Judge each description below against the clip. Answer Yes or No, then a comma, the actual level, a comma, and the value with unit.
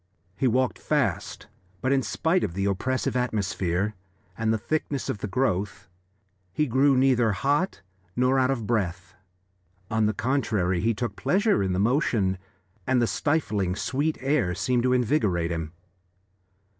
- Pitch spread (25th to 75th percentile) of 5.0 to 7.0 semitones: Yes, average, 5.3 semitones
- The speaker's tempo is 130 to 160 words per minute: Yes, average, 150 wpm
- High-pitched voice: No, low, 115 Hz